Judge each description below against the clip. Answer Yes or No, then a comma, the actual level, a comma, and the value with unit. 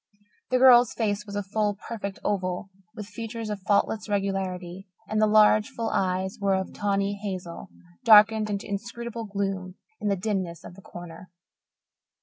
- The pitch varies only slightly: Yes, narrow, 2.1 semitones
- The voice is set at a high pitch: Yes, high, 200 Hz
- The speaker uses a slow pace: No, average, 155 wpm